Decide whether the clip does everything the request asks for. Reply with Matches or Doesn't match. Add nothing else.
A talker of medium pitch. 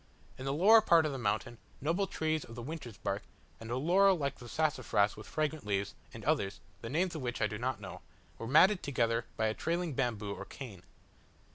Doesn't match